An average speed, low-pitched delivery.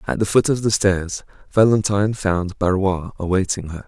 Yes: average, 170 wpm; very low, 95 Hz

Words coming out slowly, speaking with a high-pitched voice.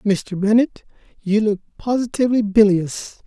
Yes: slow, 110 wpm; high, 210 Hz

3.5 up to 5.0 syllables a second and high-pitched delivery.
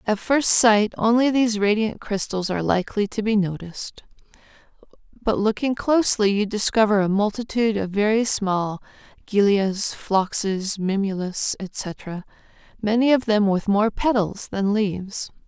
Yes: 4.6 syllables/s; high, 210 Hz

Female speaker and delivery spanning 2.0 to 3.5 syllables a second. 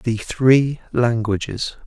No: male; 3.1 syllables/s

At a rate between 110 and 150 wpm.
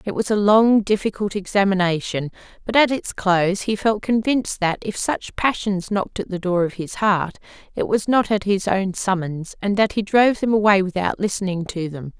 No: average, 200 wpm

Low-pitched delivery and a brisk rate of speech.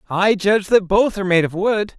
No: high, 200 Hz; fast, 240 wpm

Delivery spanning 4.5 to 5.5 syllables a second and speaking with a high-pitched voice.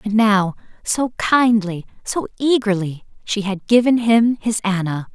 No: 4.1 syllables/s; high, 215 Hz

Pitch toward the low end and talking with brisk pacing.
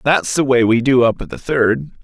Yes: low, 125 Hz; fast, 265 wpm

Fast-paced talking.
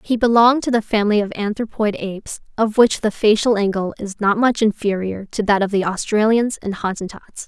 No: average, 195 wpm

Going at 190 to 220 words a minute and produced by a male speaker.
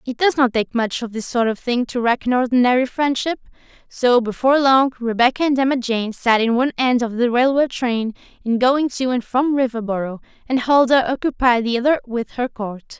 No: fast, 205 wpm; female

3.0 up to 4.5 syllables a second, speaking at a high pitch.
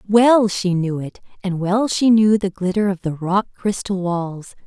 Yes: 4.2 syllables/s; high, 195 Hz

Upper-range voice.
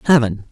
No: low, 125 Hz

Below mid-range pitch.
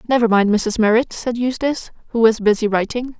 No: high, 230 Hz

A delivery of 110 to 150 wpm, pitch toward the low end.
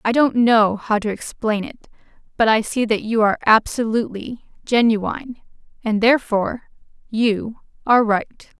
No: average, 140 wpm; high, 225 Hz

